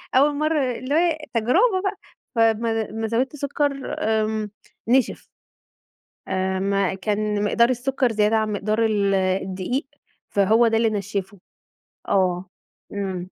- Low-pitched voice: No, high, 220 Hz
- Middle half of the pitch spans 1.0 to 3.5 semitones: No, average, 4.3 semitones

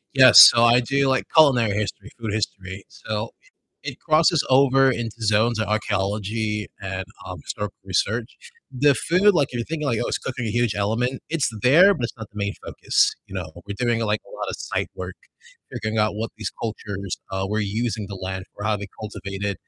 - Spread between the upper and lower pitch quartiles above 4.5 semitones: No, average, 3.5 semitones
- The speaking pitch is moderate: No, low, 110 Hz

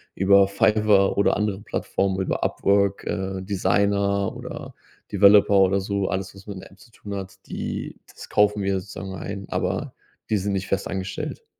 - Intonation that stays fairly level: Yes, narrow, 0.9 semitones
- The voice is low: Yes, low, 100 Hz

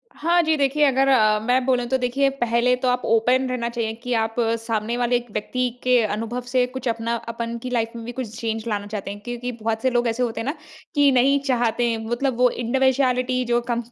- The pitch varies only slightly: Yes, narrow, 2.0 semitones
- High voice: Yes, high, 245 Hz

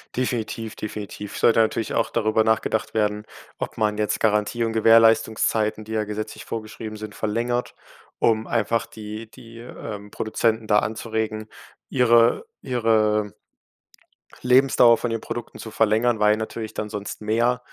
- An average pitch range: No, narrow, 1.3 semitones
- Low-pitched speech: Yes, low, 110 Hz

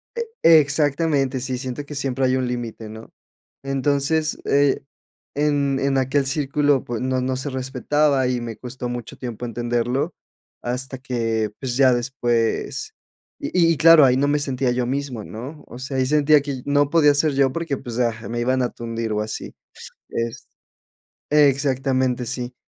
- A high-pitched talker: No, low, 130 Hz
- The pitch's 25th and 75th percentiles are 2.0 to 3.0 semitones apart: Yes, average, 2.7 semitones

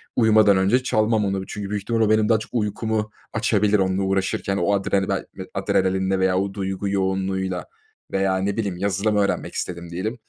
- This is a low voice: Yes, low, 100 Hz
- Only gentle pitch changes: Yes, narrow, 1.9 semitones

